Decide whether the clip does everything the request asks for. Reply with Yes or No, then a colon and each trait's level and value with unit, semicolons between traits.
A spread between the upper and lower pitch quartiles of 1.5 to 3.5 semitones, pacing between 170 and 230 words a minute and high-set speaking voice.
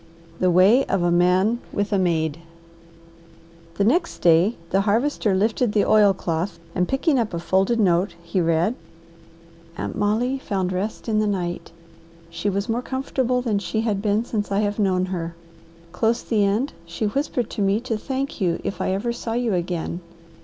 No: average, 4.0 semitones; average, 175 wpm; high, 205 Hz